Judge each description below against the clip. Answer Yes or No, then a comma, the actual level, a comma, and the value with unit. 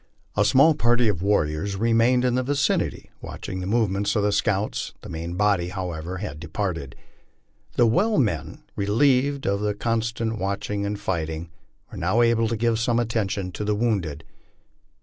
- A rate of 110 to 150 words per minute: No, average, 165 wpm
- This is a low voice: Yes, low, 105 Hz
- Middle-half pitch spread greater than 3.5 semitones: Yes, average, 4.0 semitones